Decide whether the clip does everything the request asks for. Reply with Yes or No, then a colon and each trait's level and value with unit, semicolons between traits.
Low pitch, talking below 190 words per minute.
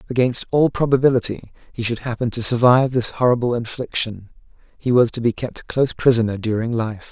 Yes: low, 120 Hz; average, 175 wpm